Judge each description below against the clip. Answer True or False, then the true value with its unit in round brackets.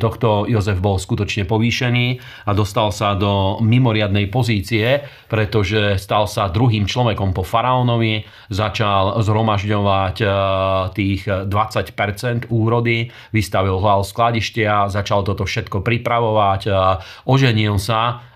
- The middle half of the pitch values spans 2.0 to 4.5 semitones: True (2.5 semitones)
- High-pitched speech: False (110 Hz)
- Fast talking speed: False (105 wpm)